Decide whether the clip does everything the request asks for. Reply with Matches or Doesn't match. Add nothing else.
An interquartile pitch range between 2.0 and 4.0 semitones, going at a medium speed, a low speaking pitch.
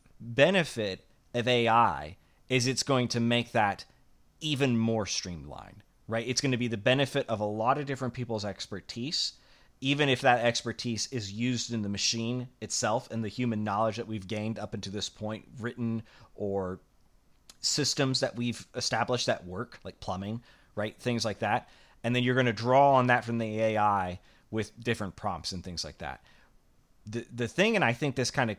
Matches